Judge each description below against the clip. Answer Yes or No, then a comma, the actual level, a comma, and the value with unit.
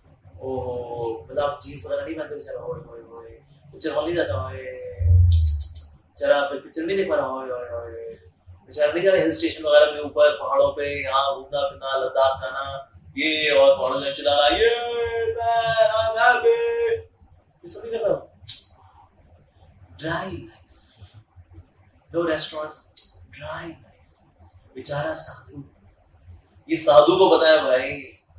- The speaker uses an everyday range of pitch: No, wide, 9.0 semitones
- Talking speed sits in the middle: No, slow, 30 wpm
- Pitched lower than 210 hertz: Yes, low, 135 Hz